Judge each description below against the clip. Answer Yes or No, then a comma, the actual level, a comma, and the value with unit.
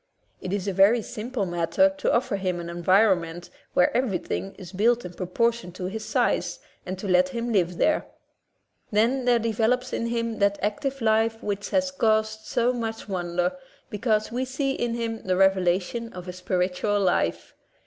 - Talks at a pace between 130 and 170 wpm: No, average, 180 wpm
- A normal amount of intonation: Yes, average, 4.2 semitones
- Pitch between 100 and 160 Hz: No, high, 210 Hz